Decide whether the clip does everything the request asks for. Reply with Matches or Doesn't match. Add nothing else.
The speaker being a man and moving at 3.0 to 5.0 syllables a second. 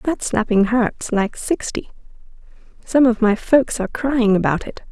Doesn't match